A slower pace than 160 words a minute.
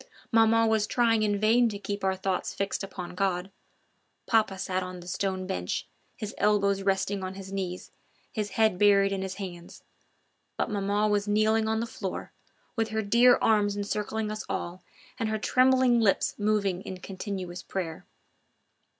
No: average, 165 wpm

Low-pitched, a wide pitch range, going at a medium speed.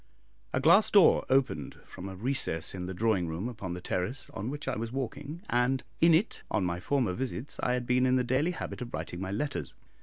No: low, 120 Hz; wide, 6.0 semitones; fast, 220 wpm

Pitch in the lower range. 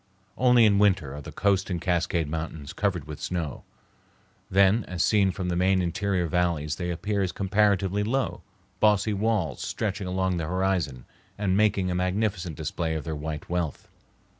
Yes: very low, 90 Hz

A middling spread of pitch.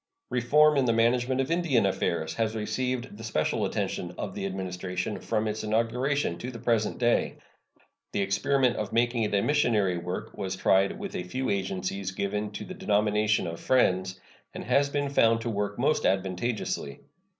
Yes: average, 4.4 semitones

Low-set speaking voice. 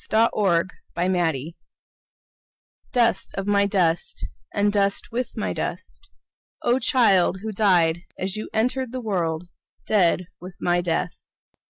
No: high, 195 Hz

